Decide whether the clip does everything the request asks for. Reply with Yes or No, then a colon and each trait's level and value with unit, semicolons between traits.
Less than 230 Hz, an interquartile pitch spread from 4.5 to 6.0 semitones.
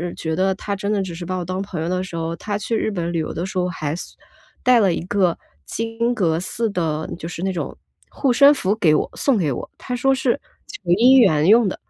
Yes: high, 190 Hz; average, 5.0 semitones